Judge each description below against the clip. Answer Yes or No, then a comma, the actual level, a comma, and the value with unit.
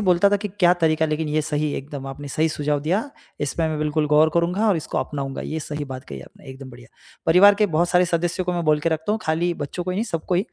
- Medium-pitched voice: Yes, medium, 160 Hz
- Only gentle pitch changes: No, average, 3.2 semitones